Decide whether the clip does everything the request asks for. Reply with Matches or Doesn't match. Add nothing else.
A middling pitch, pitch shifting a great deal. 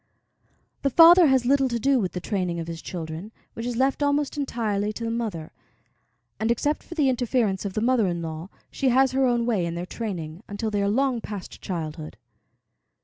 Doesn't match